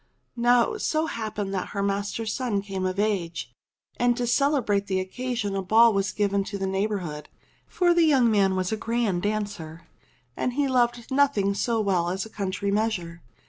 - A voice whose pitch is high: Yes, high, 205 Hz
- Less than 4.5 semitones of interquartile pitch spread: Yes, average, 3.7 semitones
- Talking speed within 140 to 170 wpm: No, average, 180 wpm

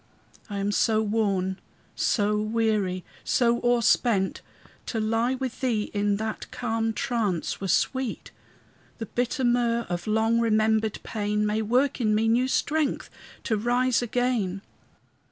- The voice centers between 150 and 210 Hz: No, high, 220 Hz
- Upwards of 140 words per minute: No, slow, 135 wpm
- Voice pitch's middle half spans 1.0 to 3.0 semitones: Yes, narrow, 2.5 semitones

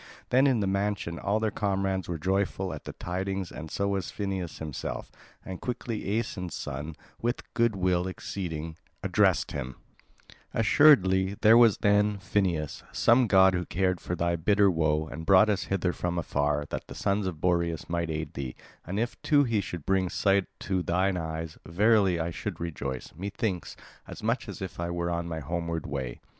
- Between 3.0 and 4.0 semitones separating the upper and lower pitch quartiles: Yes, average, 3.3 semitones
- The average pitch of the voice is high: No, very low, 95 Hz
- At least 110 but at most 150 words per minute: No, average, 180 wpm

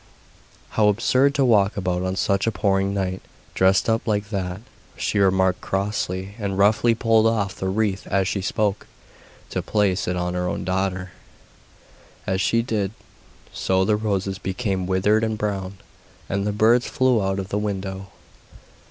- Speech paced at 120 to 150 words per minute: No, average, 160 wpm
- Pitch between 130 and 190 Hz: No, low, 100 Hz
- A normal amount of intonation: No, narrow, 2.2 semitones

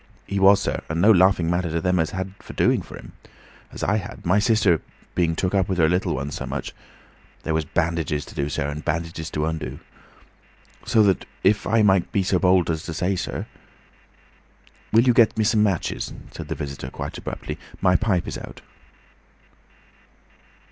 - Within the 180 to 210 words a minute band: Yes, average, 190 wpm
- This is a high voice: No, very low, 90 Hz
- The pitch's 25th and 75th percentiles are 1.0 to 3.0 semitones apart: No, average, 3.6 semitones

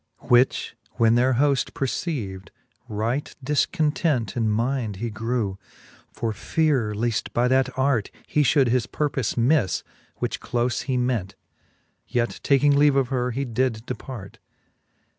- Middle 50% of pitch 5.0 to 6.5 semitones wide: No, average, 3.3 semitones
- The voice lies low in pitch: Yes, low, 125 Hz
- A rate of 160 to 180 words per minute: No, slow, 135 wpm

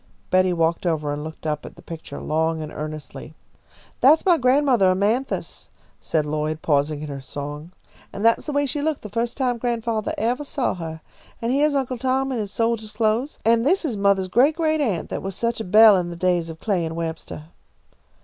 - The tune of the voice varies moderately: No, wide, 7.6 semitones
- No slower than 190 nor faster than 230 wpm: Yes, fast, 205 wpm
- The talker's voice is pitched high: Yes, high, 205 Hz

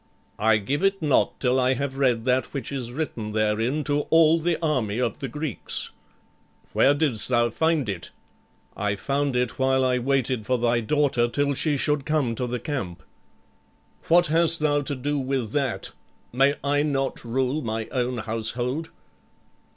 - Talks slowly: No, average, 165 wpm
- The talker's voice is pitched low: Yes, low, 130 Hz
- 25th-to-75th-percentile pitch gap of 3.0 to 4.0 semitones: Yes, average, 3.6 semitones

